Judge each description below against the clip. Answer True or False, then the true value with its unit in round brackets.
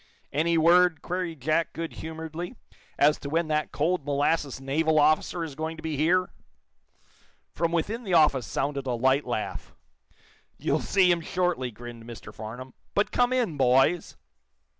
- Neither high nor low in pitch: True (155 Hz)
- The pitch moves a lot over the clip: False (3.8 semitones)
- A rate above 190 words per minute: False (155 wpm)